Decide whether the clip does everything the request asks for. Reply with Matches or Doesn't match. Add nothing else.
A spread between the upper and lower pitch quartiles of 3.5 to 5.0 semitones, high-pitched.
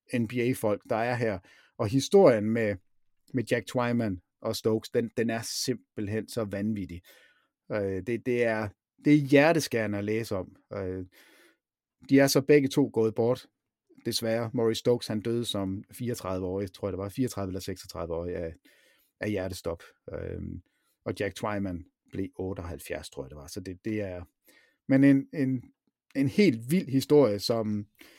Doesn't match